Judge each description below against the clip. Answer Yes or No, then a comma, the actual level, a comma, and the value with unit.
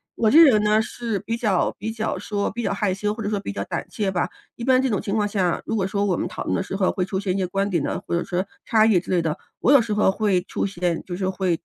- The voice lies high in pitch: Yes, high, 200 Hz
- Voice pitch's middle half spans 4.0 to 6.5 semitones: No, average, 2.8 semitones